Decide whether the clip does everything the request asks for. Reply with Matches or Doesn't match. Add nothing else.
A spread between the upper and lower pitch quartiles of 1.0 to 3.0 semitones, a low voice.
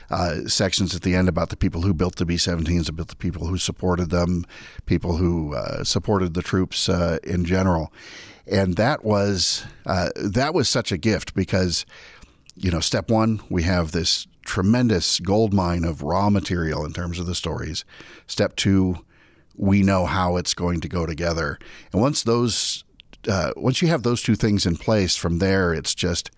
Matches